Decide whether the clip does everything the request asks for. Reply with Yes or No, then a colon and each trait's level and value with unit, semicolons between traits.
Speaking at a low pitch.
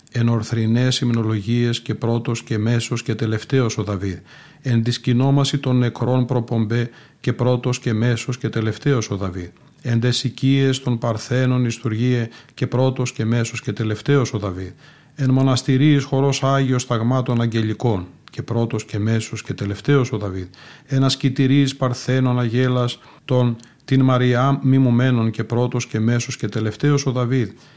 Yes: low, 125 Hz